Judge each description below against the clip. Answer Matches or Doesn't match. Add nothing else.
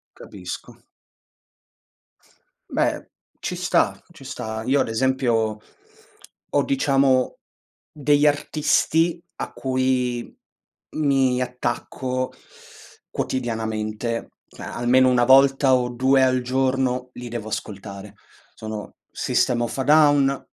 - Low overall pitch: Matches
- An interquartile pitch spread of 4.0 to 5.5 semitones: Doesn't match